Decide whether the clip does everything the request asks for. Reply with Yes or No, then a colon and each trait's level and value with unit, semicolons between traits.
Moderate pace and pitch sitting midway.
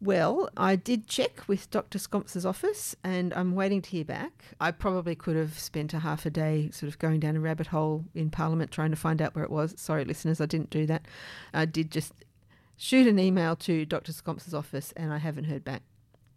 No: fast, 220 wpm; medium, 160 Hz